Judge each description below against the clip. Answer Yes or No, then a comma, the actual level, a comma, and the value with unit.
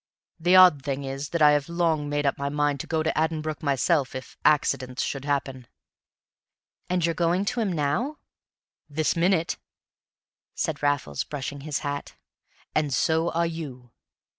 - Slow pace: No, average, 160 wpm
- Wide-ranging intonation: No, average, 3.0 semitones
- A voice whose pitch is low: No, medium, 150 Hz